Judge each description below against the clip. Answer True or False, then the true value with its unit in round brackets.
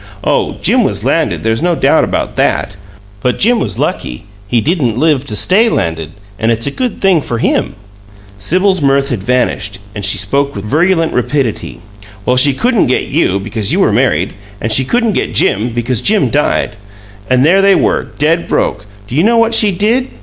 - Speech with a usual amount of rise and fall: False (8.8 semitones)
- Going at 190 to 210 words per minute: True (195 wpm)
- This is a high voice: False (135 Hz)